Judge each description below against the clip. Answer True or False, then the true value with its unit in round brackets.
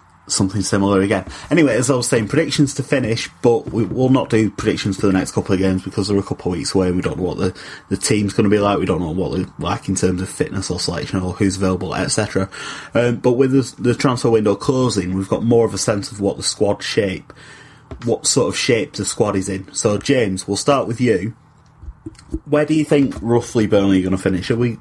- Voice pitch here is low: True (105 Hz)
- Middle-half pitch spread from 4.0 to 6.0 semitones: True (4.4 semitones)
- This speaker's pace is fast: True (250 wpm)